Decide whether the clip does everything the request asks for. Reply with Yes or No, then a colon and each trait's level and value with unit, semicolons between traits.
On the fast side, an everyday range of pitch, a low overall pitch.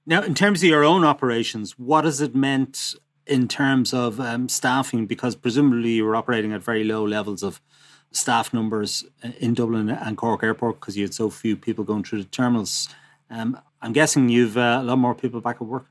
Yes: fast, 210 wpm; average, 3.4 semitones; low, 120 Hz